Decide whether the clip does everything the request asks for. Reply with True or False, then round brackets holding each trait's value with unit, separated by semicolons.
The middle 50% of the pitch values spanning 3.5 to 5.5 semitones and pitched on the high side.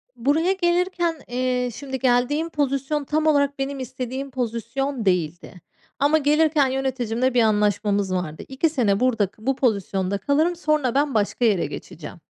True (4.7 semitones; 260 Hz)